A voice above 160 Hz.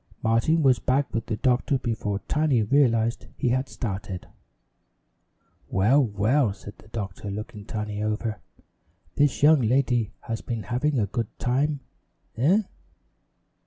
No: low, 120 Hz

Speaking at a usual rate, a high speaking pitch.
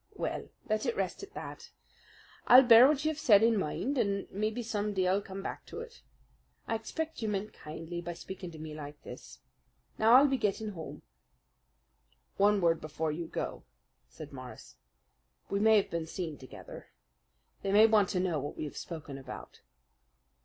Yes: average, 180 wpm; high, 200 Hz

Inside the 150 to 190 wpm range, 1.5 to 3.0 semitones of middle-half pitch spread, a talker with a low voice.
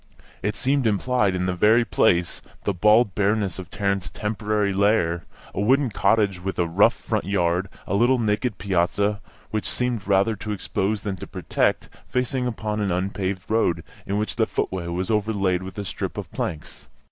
Yes: average, 175 wpm; average, 2.7 semitones; low, 100 Hz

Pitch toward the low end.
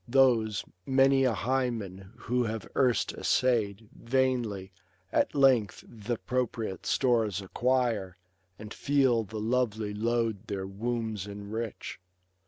Yes: low, 115 Hz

